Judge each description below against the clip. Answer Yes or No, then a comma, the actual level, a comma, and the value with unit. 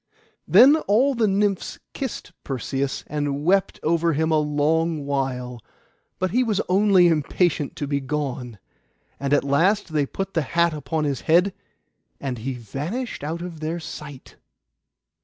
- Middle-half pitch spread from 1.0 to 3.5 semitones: No, average, 4.9 semitones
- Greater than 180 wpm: No, average, 150 wpm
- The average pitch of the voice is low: No, medium, 155 Hz